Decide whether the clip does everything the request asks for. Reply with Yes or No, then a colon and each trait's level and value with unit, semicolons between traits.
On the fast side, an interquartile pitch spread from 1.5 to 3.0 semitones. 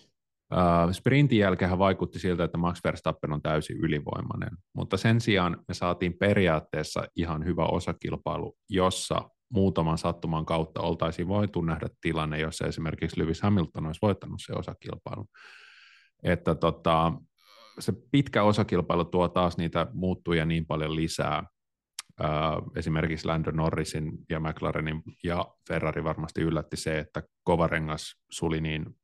No: average, 125 wpm; narrow, 2.6 semitones